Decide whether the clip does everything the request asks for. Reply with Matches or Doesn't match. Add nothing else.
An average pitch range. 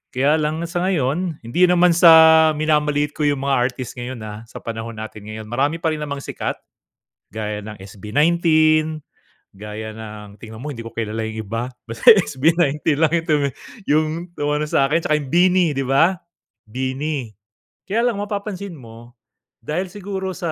Doesn't match